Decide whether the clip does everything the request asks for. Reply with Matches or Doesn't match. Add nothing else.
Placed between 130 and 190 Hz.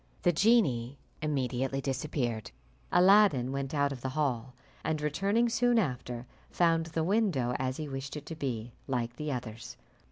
Matches